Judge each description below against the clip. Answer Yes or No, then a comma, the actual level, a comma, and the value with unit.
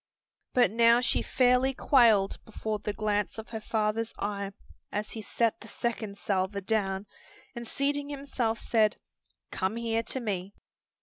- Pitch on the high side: Yes, high, 220 Hz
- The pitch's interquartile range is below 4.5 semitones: Yes, narrow, 2.5 semitones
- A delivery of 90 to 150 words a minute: Yes, average, 145 wpm